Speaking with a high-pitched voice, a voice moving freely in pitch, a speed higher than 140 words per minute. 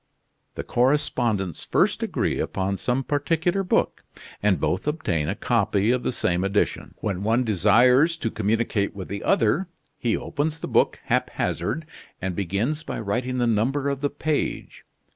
No: low, 120 Hz; wide, 6.3 semitones; average, 155 wpm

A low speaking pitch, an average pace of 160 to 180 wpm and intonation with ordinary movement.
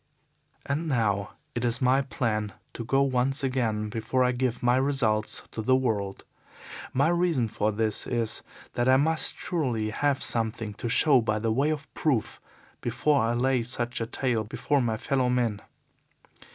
Yes: low, 120 Hz; average, 165 wpm; average, 3.3 semitones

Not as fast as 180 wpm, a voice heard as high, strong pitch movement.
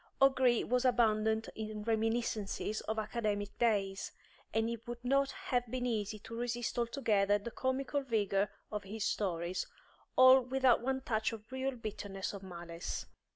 No: average, 150 wpm; high, 225 Hz; average, 3.2 semitones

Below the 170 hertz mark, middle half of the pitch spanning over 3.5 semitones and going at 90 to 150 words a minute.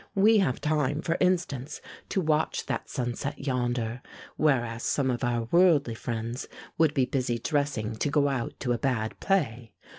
No: low, 135 Hz; average, 4.2 semitones; average, 160 wpm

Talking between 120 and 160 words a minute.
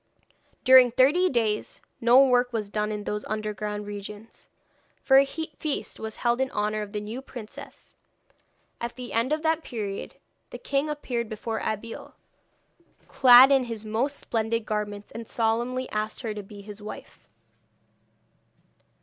Yes: average, 150 wpm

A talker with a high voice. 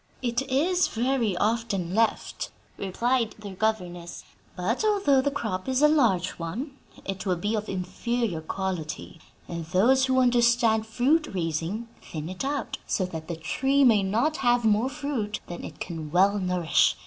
Yes: high, 220 Hz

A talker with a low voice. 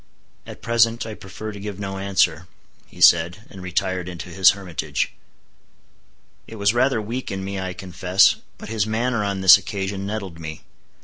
Yes: very low, 95 Hz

